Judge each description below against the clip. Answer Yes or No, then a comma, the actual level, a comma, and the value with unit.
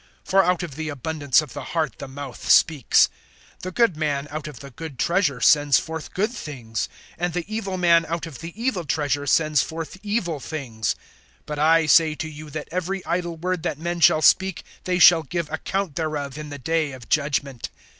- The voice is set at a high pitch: No, medium, 160 Hz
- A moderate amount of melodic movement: Yes, average, 3.2 semitones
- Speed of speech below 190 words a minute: No, average, 195 wpm